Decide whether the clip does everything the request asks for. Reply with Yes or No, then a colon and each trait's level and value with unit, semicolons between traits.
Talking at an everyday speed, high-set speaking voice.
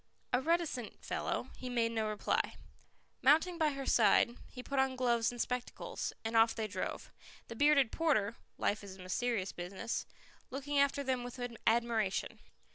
Yes: average, 160 wpm; high, 245 Hz